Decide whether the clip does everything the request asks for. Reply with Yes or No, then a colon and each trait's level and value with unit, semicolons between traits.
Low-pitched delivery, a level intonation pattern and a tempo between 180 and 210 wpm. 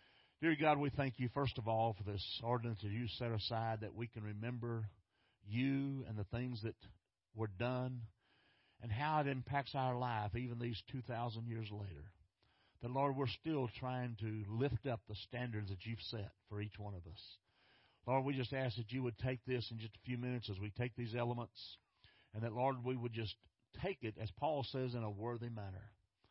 No: low, 115 Hz; average, 3.2 semitones; fast, 205 wpm